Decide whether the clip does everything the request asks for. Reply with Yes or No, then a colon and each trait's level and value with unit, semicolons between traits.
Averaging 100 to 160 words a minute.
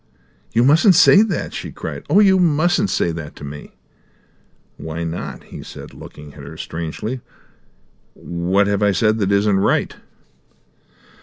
Yes: average, 150 wpm